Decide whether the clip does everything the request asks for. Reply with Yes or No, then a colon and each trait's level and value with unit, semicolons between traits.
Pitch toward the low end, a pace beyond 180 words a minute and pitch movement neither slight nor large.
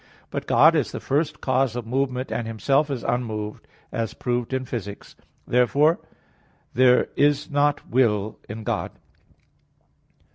No: low, 125 Hz; average, 145 wpm; average, 3.5 semitones